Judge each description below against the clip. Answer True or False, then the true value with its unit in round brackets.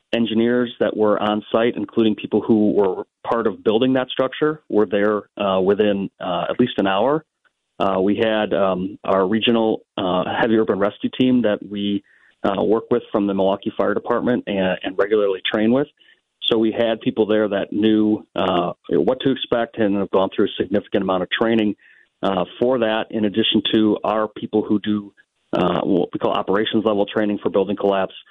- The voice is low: True (110 Hz)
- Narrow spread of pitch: True (2.3 semitones)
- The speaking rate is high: False (190 wpm)